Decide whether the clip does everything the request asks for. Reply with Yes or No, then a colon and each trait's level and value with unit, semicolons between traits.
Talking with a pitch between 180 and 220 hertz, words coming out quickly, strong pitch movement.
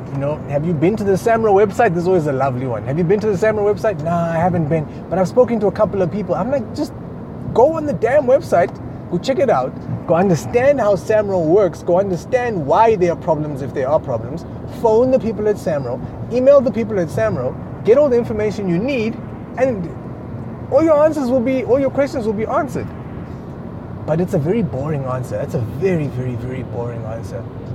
Yes: medium, 185 Hz; fast, 220 wpm; wide, 7.1 semitones